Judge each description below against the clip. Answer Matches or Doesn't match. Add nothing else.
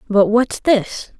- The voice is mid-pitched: Doesn't match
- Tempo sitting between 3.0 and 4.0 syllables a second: Matches